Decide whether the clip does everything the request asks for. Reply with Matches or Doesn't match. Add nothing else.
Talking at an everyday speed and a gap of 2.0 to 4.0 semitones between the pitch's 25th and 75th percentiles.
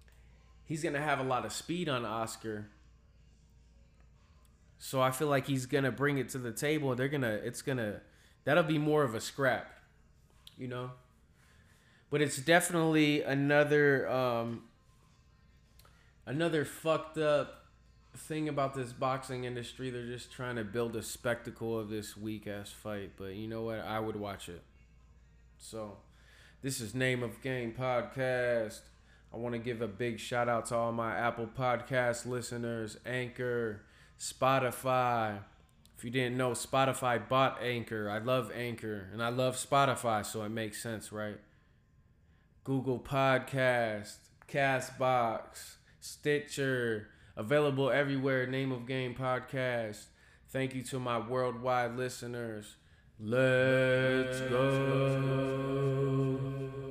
Doesn't match